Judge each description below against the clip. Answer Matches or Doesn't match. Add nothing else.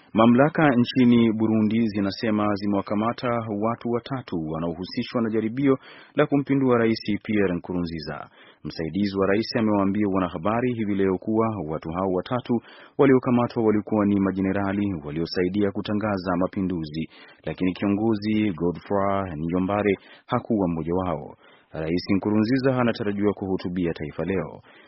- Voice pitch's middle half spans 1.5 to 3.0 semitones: Doesn't match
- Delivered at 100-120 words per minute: Matches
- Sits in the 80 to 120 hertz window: Matches